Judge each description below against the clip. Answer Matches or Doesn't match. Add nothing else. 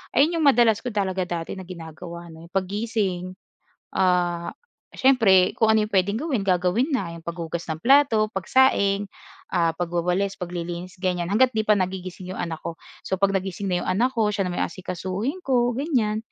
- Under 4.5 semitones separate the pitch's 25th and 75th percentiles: Matches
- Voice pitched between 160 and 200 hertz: Matches